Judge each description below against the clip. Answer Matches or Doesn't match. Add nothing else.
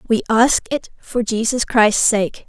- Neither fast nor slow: Matches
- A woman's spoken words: Matches